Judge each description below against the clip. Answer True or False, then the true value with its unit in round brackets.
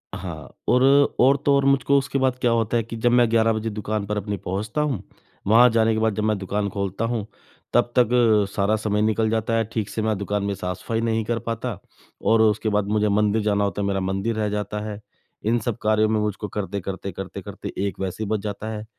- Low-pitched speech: True (110 Hz)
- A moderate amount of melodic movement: False (2.0 semitones)